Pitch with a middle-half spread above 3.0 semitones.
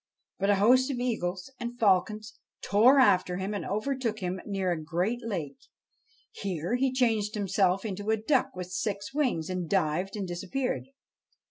Yes: average, 4.4 semitones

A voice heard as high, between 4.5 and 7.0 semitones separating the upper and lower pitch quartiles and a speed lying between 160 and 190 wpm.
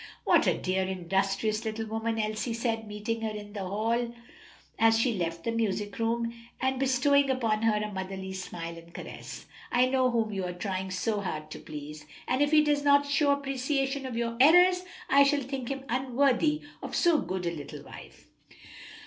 Yes: high, 225 Hz; wide, 5.5 semitones; average, 185 wpm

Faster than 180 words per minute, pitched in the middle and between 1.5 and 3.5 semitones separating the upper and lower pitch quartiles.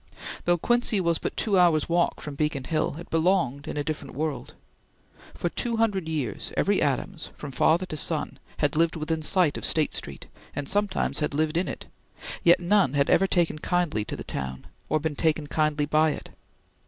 Yes: average, 190 wpm; medium, 160 Hz; average, 3.2 semitones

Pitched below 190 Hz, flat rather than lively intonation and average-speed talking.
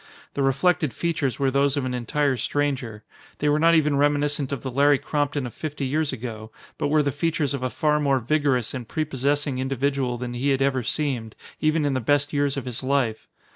No: medium, 140 Hz; narrow, 2.3 semitones; fast, 210 wpm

